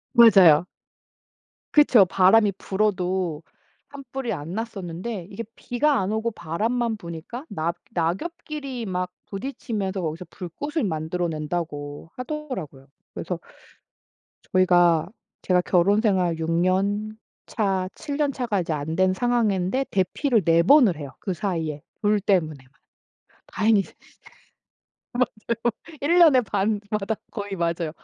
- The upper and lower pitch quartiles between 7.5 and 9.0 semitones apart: No, average, 5.3 semitones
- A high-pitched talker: Yes, high, 195 Hz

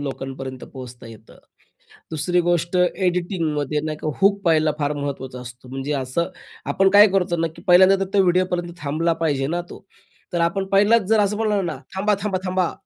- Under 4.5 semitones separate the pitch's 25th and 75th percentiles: No, average, 4.9 semitones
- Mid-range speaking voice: Yes, medium, 170 Hz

